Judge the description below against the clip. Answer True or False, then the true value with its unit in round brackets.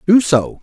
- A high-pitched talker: False (170 Hz)